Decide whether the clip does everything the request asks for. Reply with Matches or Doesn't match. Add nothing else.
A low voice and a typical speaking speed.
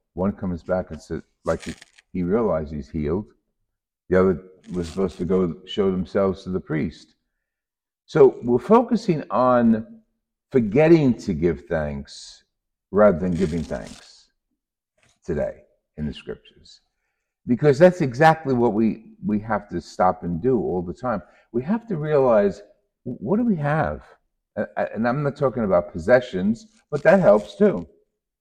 Matches